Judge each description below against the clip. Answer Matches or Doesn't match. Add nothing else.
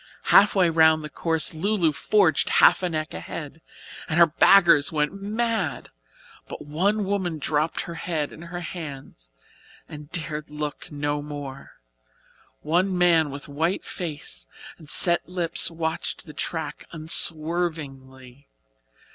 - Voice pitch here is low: Doesn't match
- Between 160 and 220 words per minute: Doesn't match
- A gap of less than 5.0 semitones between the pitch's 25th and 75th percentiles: Matches